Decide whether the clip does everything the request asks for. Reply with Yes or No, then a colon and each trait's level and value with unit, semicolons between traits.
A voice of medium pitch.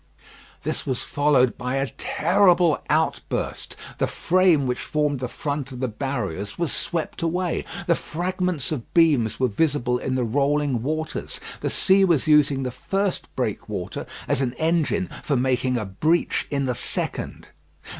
Yes: medium, 145 Hz